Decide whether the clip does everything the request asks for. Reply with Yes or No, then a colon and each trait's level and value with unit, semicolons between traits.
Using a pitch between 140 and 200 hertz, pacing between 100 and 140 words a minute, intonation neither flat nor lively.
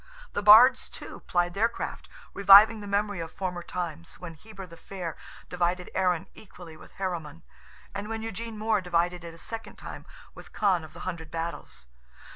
No: medium, 185 Hz; average, 175 wpm; average, 3.4 semitones